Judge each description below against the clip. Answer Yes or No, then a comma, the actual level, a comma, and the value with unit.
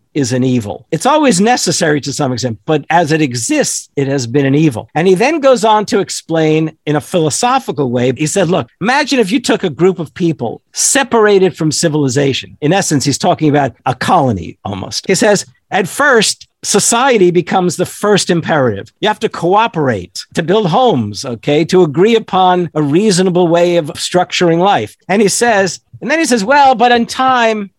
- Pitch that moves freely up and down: Yes, wide, 6.3 semitones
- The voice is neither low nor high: Yes, medium, 175 Hz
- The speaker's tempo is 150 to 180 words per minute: No, average, 190 wpm